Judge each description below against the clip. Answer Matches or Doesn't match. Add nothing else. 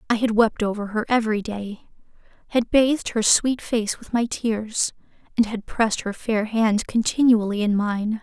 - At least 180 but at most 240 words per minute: Doesn't match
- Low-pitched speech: Doesn't match